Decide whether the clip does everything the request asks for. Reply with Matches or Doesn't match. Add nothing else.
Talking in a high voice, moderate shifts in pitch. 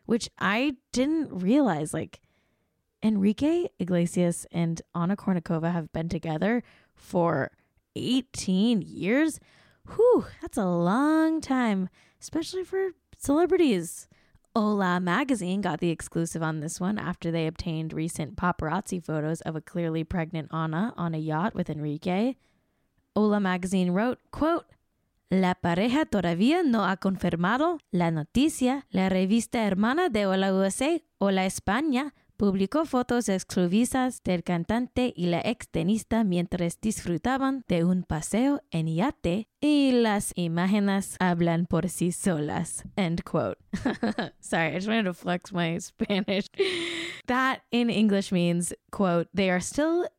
Doesn't match